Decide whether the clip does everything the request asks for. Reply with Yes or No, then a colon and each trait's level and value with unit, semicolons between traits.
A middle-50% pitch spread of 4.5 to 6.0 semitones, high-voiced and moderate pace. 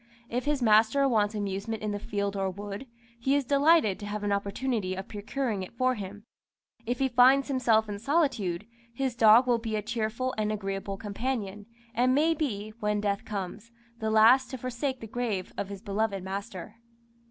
No: average, 3.9 semitones; high, 220 Hz; average, 180 wpm